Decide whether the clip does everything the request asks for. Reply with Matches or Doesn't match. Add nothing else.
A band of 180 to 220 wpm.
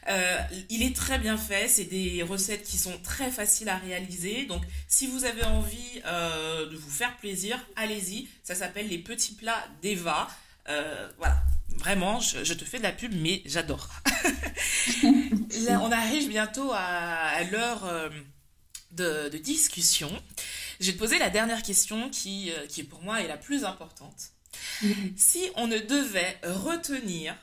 Doesn't match